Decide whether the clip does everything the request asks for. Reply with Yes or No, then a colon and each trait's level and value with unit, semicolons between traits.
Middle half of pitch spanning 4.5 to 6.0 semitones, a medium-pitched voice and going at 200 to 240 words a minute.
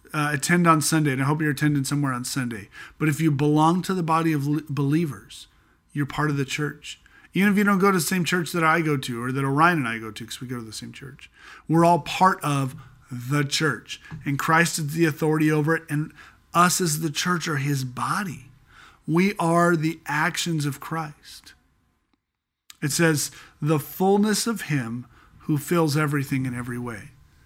No: average, 3.1 semitones; medium, 150 Hz; fast, 205 wpm